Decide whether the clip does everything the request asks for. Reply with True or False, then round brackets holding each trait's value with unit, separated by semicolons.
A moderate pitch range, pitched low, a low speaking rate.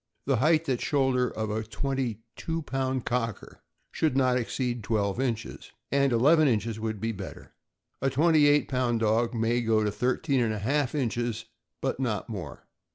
False (3.4 semitones; 125 Hz; 170 wpm)